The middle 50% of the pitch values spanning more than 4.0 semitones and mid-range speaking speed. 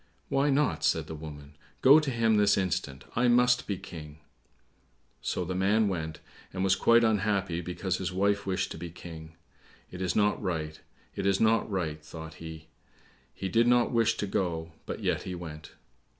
Yes: average, 5.1 semitones; average, 180 wpm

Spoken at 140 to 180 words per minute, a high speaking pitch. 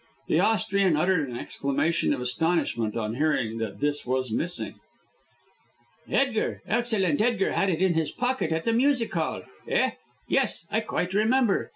No: average, 155 wpm; medium, 175 Hz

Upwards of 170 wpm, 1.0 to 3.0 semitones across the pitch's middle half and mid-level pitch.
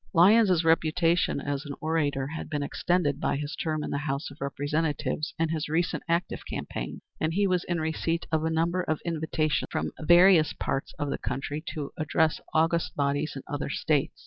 Yes: average, 185 wpm; narrow, 2.5 semitones; medium, 155 Hz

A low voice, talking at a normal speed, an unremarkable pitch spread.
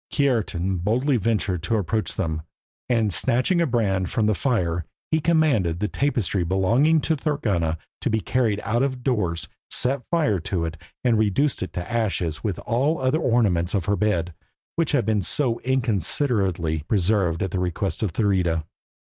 No: low, 105 Hz; average, 170 wpm; wide, 6.1 semitones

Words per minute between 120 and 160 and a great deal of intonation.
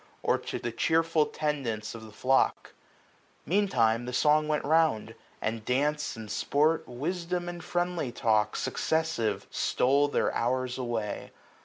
Yes: average, 140 wpm; wide, 5.7 semitones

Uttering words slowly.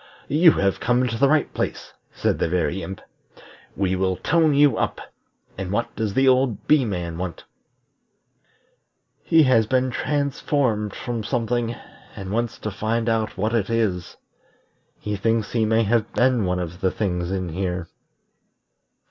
No: average, 155 wpm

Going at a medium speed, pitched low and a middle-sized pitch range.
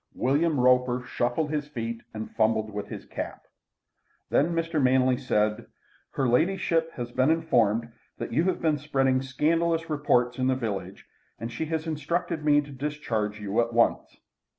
Yes: average, 160 wpm; low, 130 Hz; average, 4.8 semitones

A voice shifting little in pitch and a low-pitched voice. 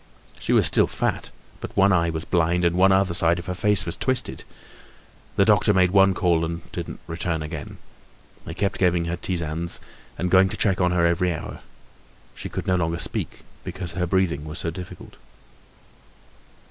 Yes: narrow, 2.0 semitones; very low, 90 Hz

